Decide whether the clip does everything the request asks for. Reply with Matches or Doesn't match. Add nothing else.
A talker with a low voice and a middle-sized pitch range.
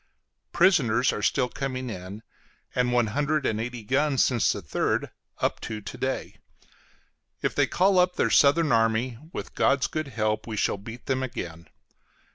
Matches